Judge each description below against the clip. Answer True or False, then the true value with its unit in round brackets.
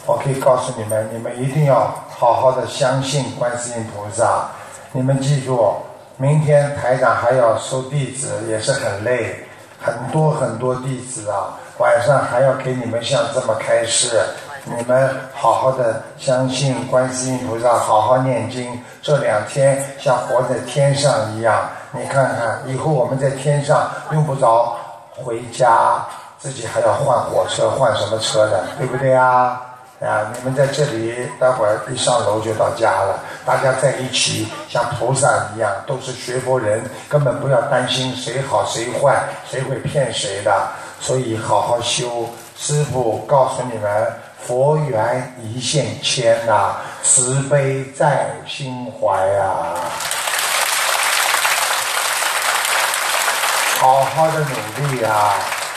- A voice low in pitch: True (130 Hz)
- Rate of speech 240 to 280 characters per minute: False (205 characters per minute)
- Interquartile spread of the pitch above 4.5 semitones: False (2.6 semitones)